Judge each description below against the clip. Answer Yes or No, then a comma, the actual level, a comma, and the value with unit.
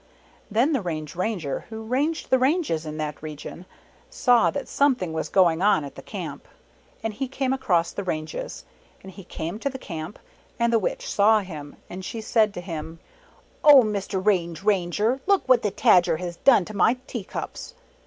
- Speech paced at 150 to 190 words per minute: Yes, average, 185 wpm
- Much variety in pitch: Yes, wide, 6.7 semitones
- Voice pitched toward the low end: No, high, 205 Hz